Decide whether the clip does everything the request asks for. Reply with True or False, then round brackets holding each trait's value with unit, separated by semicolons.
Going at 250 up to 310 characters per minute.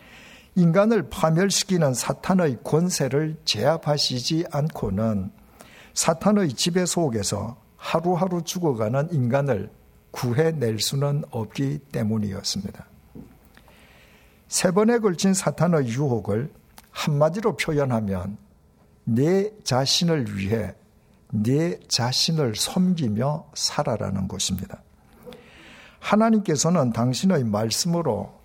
False (230 characters per minute)